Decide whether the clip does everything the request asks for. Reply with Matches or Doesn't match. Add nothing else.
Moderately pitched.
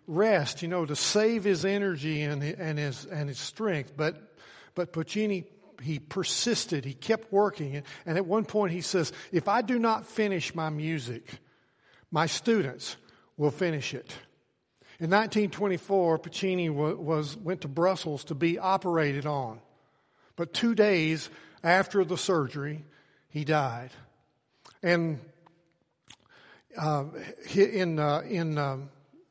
Matches